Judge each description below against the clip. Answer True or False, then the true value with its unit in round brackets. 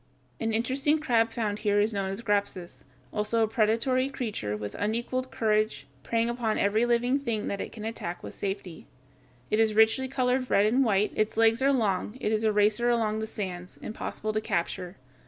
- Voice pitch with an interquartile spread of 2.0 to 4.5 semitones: True (2.5 semitones)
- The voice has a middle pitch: False (220 Hz)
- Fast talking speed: False (190 wpm)